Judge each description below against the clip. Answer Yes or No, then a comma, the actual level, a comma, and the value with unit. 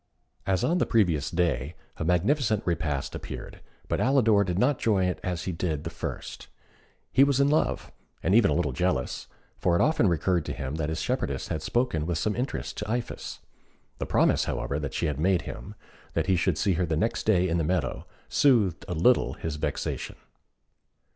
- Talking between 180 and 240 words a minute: Yes, average, 195 wpm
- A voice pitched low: Yes, very low, 90 Hz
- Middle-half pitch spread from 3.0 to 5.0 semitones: No, wide, 5.4 semitones